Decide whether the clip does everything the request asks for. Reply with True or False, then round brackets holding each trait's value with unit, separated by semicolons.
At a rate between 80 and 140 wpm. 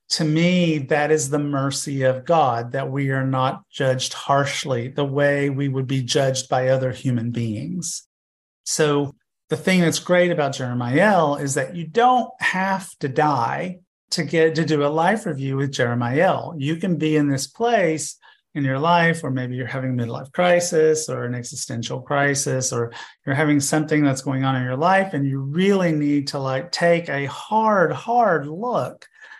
False (185 wpm)